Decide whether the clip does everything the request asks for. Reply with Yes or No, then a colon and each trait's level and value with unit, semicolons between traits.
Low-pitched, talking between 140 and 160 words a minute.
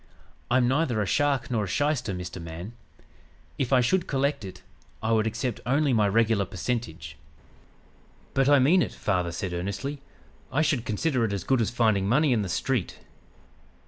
No: low, 115 Hz; average, 175 wpm